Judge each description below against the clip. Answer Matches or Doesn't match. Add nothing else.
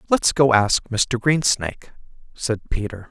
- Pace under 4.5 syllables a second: Matches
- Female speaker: Doesn't match